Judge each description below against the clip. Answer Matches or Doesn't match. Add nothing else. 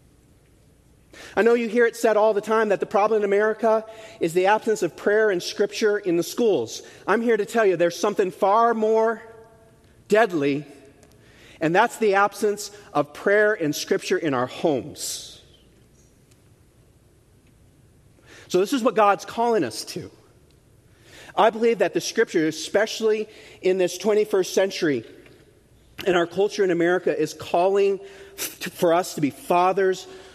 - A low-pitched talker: Doesn't match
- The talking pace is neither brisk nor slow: Matches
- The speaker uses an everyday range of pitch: Matches